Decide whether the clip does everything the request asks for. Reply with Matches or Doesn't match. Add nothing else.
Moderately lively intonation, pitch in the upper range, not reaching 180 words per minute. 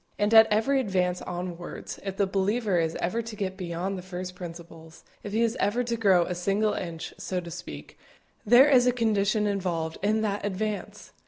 Doesn't match